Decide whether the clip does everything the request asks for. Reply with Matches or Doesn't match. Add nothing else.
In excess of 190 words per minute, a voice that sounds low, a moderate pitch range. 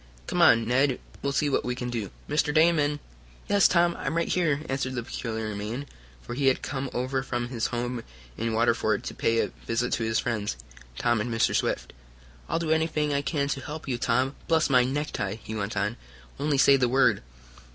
Matches